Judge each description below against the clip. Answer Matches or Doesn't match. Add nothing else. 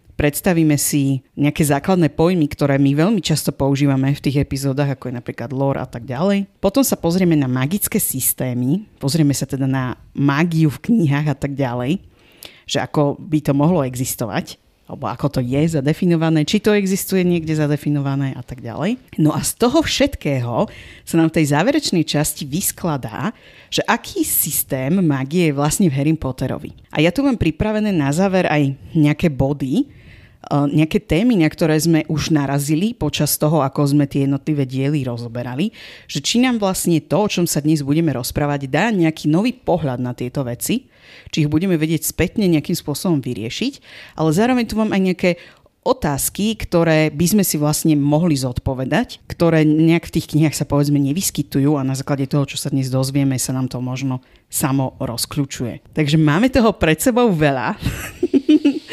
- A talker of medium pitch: Matches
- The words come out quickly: Matches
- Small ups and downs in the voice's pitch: Doesn't match